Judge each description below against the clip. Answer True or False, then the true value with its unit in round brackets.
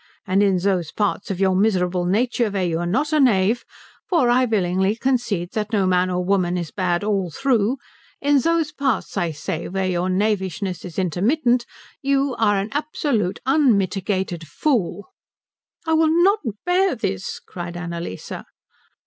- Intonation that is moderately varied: False (5.8 semitones)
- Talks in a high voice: True (200 Hz)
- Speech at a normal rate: True (155 wpm)